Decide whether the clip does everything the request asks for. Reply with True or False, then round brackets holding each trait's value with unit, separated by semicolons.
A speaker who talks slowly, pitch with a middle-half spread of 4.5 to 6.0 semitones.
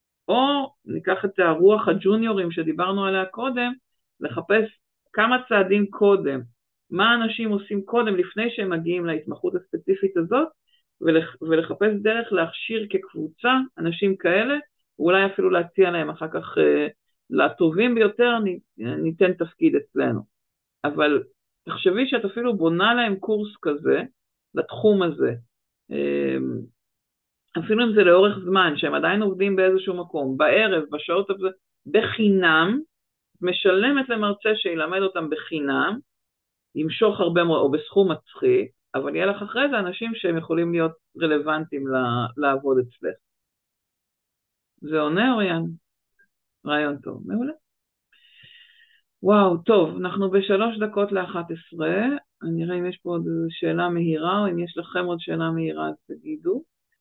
False (125 wpm; 5.1 semitones)